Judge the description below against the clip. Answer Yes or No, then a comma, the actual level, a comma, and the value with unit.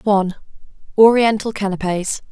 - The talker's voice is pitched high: Yes, high, 205 Hz